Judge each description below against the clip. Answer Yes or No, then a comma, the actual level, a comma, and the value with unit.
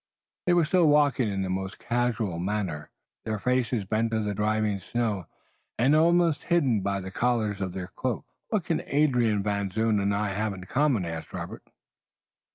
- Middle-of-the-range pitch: No, low, 110 Hz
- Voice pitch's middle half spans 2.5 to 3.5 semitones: No, average, 4.2 semitones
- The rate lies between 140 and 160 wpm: No, average, 175 wpm